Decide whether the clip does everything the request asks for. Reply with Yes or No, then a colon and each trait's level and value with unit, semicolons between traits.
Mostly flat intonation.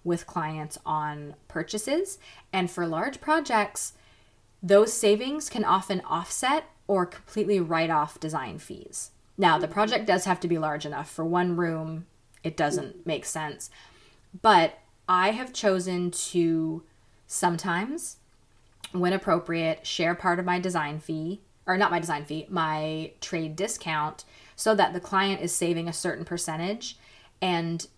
No: average, 3.5 semitones